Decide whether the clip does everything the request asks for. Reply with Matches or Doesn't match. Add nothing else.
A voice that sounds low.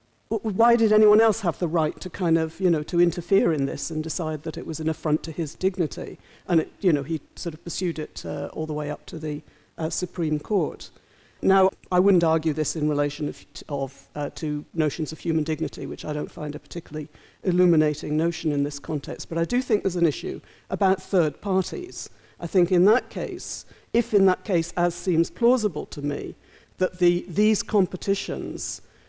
Doesn't match